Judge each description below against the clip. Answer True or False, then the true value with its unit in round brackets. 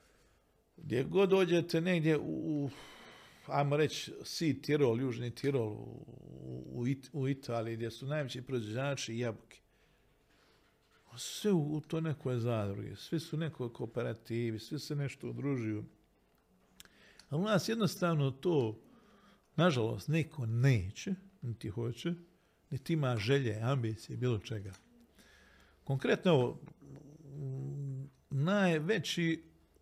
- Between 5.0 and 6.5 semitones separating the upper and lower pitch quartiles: True (5.3 semitones)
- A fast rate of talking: False (110 wpm)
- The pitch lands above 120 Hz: True (140 Hz)